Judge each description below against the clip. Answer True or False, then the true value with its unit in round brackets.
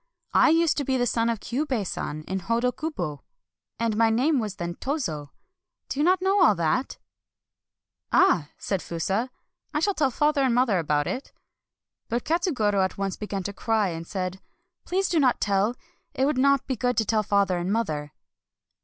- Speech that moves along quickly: True (215 wpm)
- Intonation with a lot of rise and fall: True (6.5 semitones)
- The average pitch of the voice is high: True (230 Hz)